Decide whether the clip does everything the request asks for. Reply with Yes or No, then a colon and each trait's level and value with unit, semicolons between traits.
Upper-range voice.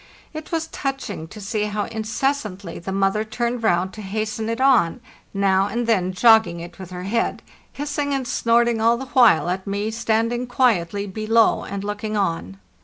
Yes: high, 215 Hz